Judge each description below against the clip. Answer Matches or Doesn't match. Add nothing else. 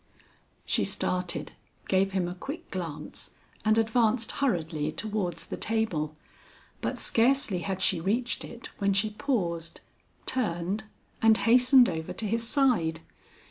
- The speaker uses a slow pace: Matches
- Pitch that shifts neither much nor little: Matches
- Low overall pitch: Doesn't match